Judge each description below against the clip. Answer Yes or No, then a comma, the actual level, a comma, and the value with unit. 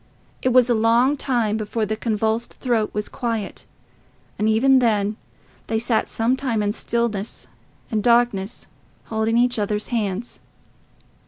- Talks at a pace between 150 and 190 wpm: No, average, 140 wpm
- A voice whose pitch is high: Yes, high, 225 Hz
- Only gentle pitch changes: Yes, narrow, 2.2 semitones